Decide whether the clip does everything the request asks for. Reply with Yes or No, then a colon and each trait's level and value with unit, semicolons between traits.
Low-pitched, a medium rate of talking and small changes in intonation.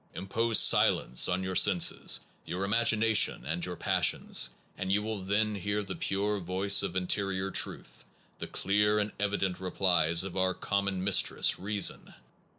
Yes: very low, 95 Hz; average, 155 wpm; narrow, 1.9 semitones